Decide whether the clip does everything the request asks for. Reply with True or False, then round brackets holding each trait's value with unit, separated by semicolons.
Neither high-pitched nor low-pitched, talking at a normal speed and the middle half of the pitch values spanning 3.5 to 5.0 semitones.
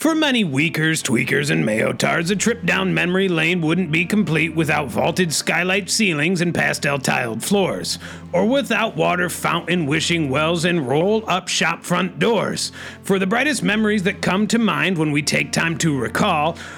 True (175 Hz; 170 wpm; 4.1 semitones)